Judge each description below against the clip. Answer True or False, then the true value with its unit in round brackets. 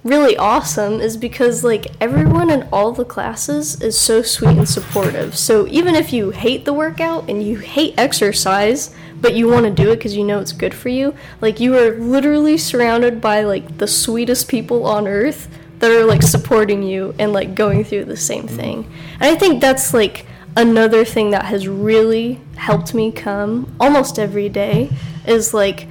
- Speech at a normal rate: True (190 wpm)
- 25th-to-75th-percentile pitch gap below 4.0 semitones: True (3.1 semitones)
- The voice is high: True (225 Hz)